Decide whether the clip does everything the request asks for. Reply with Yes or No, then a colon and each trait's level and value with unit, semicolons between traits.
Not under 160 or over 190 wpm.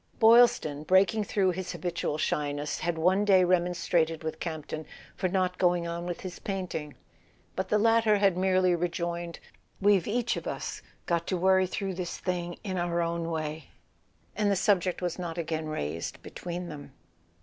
Yes: average, 170 wpm